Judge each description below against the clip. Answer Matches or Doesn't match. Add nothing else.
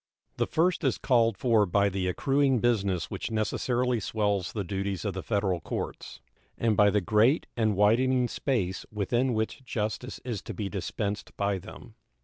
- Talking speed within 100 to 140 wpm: Doesn't match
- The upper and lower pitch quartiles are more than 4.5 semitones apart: Doesn't match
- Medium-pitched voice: Doesn't match